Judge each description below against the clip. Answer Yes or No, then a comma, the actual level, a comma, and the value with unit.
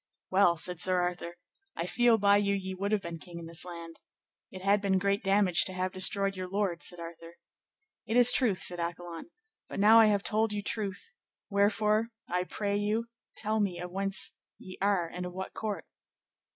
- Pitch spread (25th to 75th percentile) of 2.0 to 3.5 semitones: Yes, narrow, 2.5 semitones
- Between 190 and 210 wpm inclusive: Yes, average, 195 wpm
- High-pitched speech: Yes, high, 195 Hz